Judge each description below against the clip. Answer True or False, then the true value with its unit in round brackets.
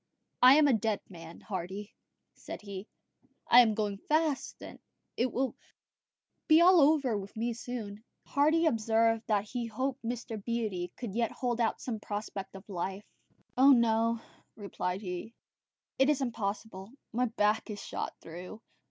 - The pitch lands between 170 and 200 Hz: False (225 Hz)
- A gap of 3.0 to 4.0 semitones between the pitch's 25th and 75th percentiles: True (3.5 semitones)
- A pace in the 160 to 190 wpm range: False (150 wpm)